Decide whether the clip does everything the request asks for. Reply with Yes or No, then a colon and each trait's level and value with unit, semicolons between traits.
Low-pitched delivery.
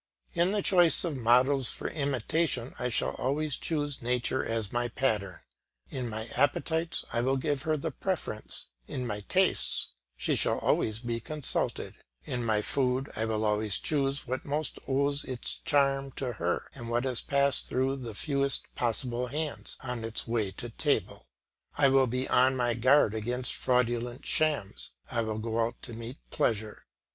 Yes: low, 125 Hz